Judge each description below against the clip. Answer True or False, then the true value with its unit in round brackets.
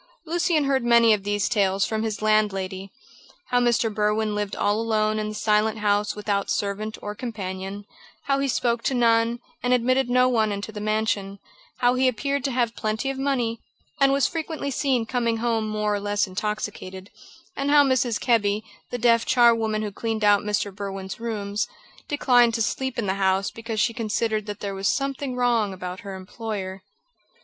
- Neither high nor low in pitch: False (220 Hz)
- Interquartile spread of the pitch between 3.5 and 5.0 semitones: False (2.9 semitones)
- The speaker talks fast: False (180 wpm)